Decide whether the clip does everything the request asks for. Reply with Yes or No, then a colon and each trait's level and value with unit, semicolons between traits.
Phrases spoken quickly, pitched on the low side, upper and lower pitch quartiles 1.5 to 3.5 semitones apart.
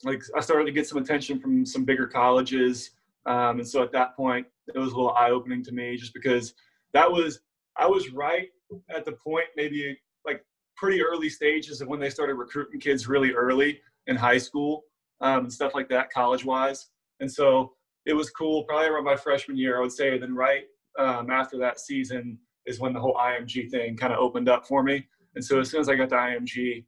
Yes: fast, 215 wpm; low, 130 Hz; average, 2.8 semitones